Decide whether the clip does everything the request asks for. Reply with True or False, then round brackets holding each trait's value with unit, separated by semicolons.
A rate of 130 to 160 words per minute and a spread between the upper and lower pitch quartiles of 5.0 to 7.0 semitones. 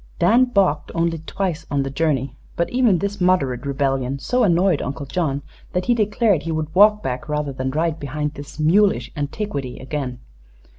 False (170 wpm; 5.3 semitones)